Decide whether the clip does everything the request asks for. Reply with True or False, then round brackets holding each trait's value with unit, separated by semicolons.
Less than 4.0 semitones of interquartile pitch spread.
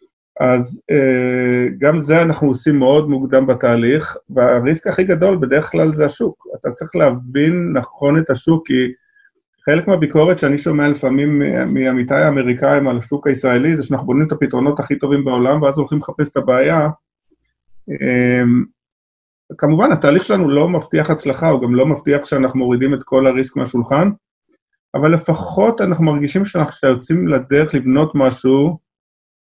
True (3.2 semitones)